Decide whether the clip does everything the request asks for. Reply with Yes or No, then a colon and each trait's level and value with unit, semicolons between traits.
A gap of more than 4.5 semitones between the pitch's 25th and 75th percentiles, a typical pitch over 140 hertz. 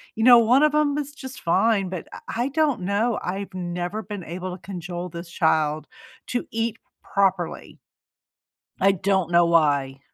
Yes: average, 5.0 semitones; high, 190 Hz